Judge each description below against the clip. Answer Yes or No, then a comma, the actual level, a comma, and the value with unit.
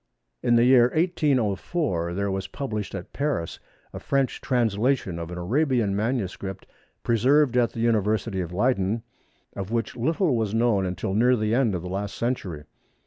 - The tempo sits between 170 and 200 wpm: No, average, 160 wpm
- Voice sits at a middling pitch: No, low, 115 Hz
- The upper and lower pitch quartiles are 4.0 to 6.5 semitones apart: Yes, average, 4.7 semitones